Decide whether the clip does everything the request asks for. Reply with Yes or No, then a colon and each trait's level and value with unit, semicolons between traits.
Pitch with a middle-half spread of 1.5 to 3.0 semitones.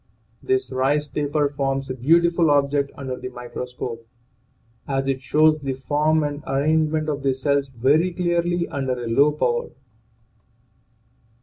Yes: average, 2.7 semitones